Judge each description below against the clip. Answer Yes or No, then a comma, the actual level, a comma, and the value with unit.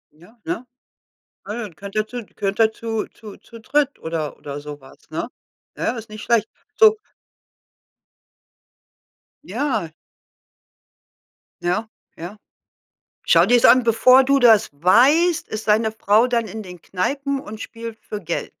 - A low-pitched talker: No, high, 220 Hz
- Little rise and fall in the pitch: No, average, 3.7 semitones